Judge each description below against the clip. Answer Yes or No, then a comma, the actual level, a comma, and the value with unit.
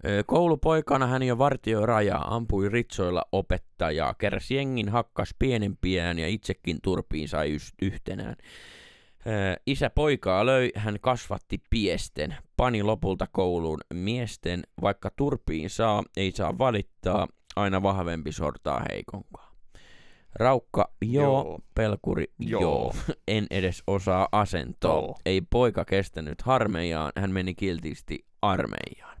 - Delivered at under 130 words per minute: Yes, average, 105 wpm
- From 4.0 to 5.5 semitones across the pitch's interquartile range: Yes, average, 4.7 semitones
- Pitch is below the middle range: Yes, low, 100 Hz